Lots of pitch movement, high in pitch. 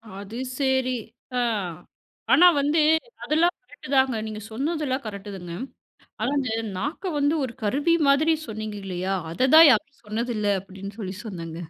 Yes: wide, 5.9 semitones; high, 240 Hz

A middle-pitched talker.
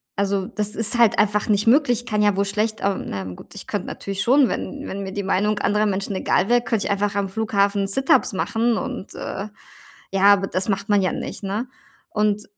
No: high, 205 Hz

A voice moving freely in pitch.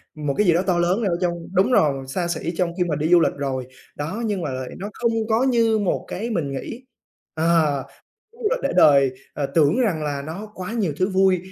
Yes: wide, 5.8 semitones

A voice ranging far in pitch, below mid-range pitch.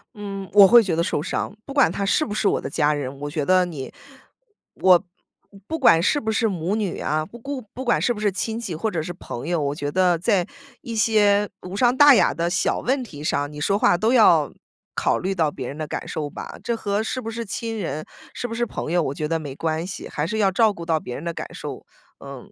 No: wide, 5.9 semitones; medium, 185 Hz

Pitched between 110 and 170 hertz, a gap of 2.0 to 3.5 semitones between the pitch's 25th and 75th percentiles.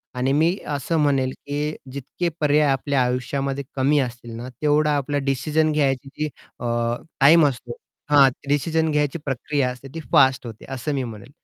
Yes: medium, 140 Hz; narrow, 2.4 semitones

